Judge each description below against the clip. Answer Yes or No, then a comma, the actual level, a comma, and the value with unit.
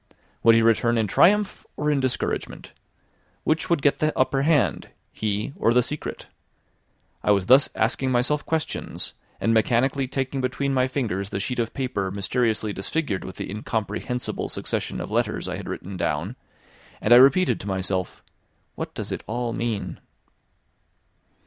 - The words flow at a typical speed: Yes, average, 155 wpm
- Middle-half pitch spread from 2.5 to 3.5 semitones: No, average, 4.5 semitones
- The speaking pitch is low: Yes, low, 120 Hz